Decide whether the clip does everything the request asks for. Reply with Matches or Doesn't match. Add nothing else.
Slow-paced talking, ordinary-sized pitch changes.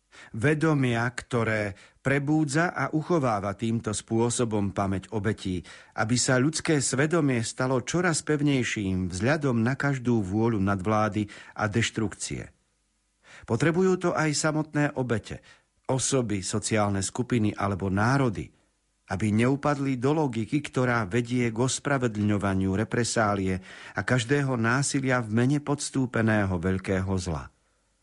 Matches